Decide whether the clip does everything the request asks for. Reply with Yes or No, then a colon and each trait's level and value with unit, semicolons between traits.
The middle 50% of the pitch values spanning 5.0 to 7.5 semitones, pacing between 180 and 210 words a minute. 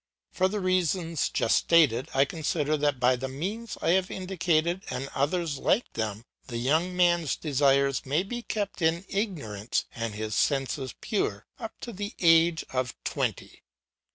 No: wide, 5.6 semitones; average, 155 wpm